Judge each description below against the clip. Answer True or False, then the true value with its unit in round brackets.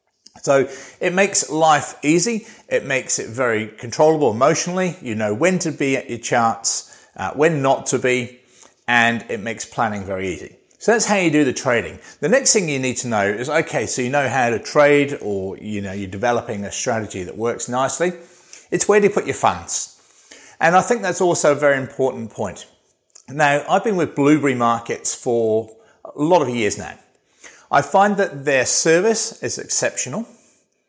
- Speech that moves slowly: False (190 wpm)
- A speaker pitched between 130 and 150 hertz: True (140 Hz)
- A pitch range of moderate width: False (6.9 semitones)